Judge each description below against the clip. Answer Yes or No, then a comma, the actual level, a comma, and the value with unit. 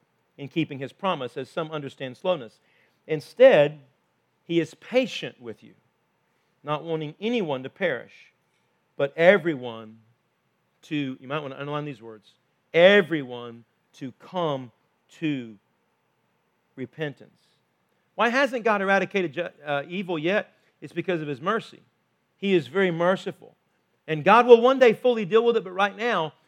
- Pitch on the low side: No, medium, 160 Hz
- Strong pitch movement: Yes, wide, 5.8 semitones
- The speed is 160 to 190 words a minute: No, average, 140 wpm